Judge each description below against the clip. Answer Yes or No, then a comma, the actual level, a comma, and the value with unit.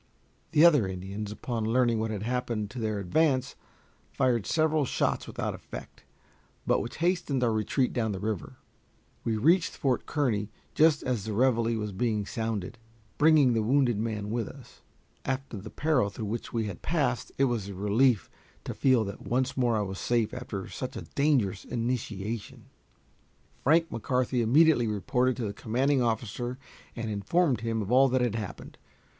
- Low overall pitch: Yes, low, 120 Hz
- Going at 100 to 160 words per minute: No, average, 170 wpm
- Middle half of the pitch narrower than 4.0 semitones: Yes, average, 3.5 semitones